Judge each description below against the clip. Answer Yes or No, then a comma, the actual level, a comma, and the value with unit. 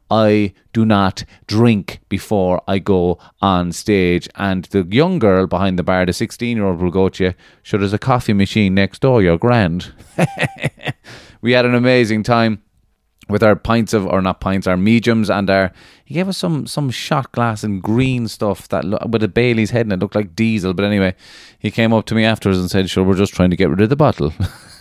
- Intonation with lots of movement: No, average, 3.3 semitones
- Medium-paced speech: No, fast, 220 wpm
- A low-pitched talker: Yes, low, 105 Hz